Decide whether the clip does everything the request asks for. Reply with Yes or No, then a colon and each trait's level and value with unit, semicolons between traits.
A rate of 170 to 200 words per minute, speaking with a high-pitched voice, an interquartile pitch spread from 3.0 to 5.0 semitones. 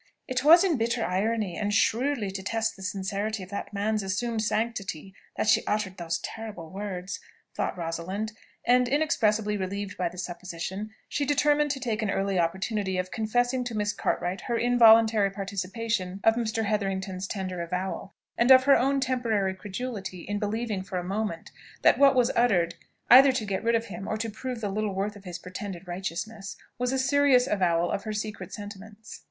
Yes: average, 180 wpm; high, 210 Hz; average, 3.5 semitones